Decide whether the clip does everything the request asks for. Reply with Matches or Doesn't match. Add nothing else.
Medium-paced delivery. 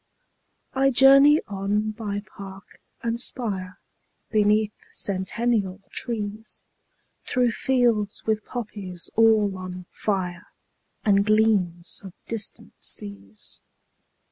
Doesn't match